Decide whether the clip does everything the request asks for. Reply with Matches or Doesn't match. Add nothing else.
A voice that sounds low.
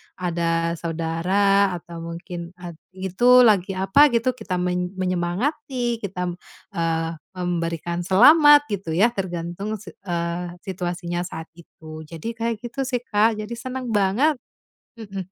Doesn't match